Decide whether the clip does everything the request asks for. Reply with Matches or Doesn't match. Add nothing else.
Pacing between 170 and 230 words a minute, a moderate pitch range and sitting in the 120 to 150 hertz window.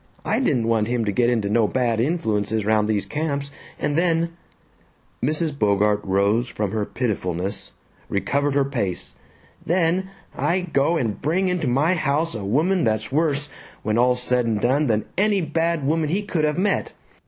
Doesn't match